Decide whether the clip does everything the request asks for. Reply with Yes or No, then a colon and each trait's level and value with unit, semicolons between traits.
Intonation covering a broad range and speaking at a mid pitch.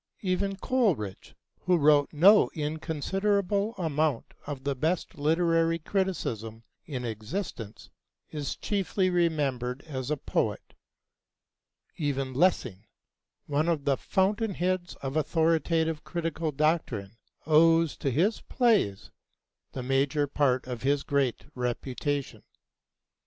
No: average, 4.8 semitones; medium, 155 Hz